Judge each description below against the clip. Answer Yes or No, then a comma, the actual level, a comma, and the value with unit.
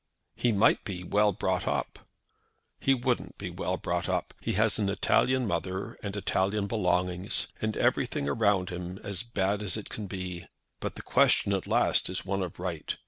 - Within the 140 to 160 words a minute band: No, average, 180 wpm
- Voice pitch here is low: Yes, low, 100 Hz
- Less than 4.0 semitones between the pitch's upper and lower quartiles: Yes, narrow, 2.5 semitones